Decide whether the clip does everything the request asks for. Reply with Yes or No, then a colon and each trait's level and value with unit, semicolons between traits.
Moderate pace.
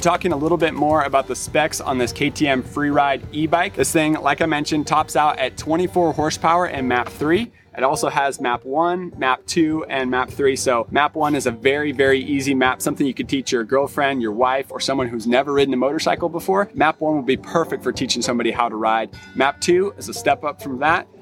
No: fast, 225 wpm